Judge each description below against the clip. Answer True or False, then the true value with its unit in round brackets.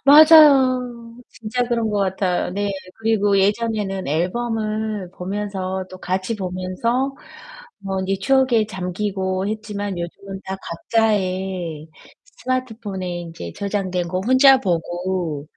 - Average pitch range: True (3.5 semitones)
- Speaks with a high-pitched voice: True (200 Hz)